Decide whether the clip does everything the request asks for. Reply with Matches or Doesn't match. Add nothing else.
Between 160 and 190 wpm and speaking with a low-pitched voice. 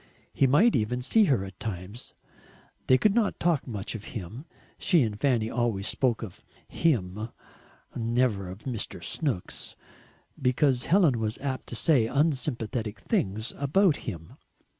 Doesn't match